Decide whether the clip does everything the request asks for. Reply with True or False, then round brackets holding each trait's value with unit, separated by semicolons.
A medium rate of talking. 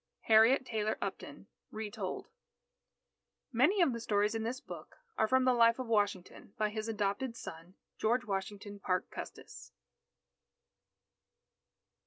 False (125 wpm)